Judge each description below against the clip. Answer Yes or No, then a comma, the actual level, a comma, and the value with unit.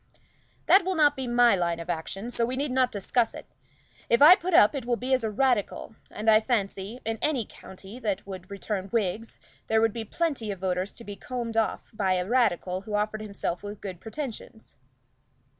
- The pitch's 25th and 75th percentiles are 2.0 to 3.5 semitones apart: No, average, 4.0 semitones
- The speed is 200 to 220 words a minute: Yes, fast, 205 wpm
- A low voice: No, high, 220 Hz